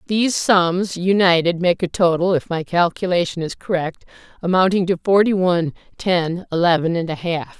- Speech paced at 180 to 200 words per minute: No, average, 160 wpm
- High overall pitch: No, medium, 175 Hz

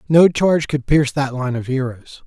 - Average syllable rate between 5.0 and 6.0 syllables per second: Yes, 5.3 syllables/s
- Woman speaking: No, male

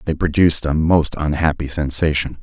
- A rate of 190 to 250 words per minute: No, average, 150 wpm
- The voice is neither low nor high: No, very low, 75 Hz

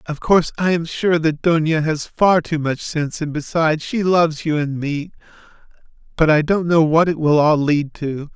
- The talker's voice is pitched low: No, medium, 155 Hz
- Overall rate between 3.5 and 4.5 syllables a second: No, 4.9 syllables/s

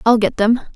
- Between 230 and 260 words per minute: Yes, fast, 240 wpm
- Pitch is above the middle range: Yes, high, 225 Hz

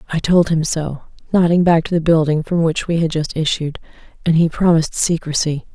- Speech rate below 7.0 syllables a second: Yes, 5.5 syllables/s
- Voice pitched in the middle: Yes, medium, 160 Hz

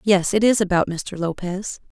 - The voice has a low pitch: No, high, 190 Hz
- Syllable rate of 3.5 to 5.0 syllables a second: Yes, 4.6 syllables/s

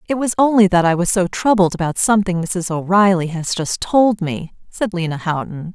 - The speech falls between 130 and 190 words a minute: No, average, 200 wpm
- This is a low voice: No, medium, 185 Hz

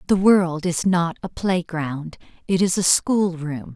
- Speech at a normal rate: Yes, average, 160 wpm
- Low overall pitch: No, medium, 175 Hz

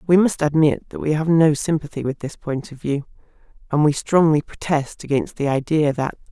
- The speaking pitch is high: No, medium, 150 Hz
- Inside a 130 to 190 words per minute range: No, average, 200 wpm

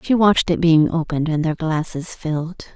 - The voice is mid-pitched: Yes, medium, 165 Hz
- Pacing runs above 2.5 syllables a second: Yes, 5.5 syllables/s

